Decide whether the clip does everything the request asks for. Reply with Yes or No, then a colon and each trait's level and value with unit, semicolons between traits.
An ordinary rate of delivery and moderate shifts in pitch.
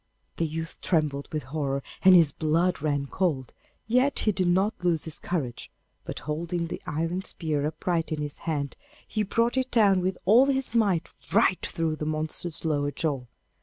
Yes: average, 175 wpm; average, 3.7 semitones